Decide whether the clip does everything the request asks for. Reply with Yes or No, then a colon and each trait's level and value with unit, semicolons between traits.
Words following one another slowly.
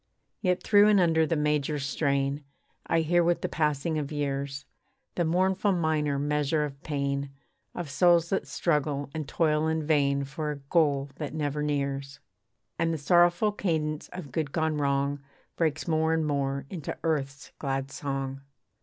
No: average, 160 wpm